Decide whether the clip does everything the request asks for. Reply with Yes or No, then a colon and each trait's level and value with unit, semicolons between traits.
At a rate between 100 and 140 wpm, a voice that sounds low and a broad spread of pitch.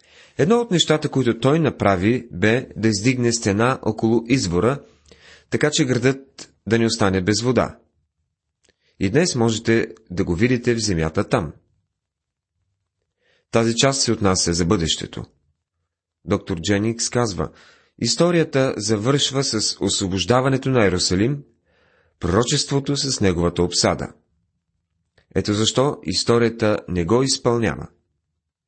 Yes: slow, 115 wpm; low, 110 Hz; wide, 5.9 semitones